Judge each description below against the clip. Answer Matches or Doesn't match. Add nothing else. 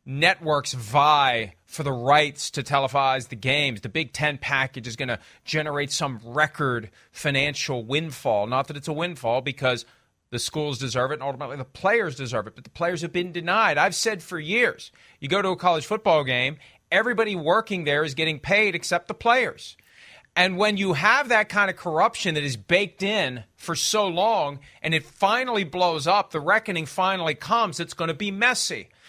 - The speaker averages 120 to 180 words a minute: Doesn't match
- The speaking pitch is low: Doesn't match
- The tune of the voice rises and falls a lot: Matches